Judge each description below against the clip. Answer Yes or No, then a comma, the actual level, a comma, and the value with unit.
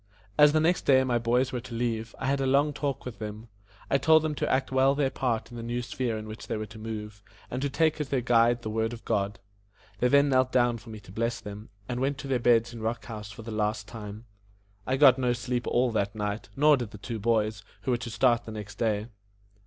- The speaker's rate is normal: No, fast, 260 wpm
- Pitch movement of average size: Yes, average, 3.2 semitones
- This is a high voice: No, low, 120 Hz